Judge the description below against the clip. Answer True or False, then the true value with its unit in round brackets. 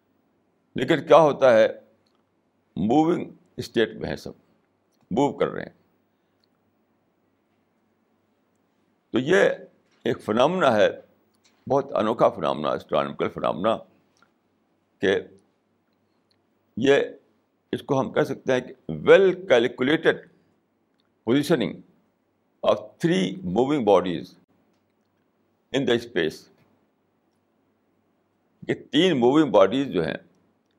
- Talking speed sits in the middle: False (95 wpm)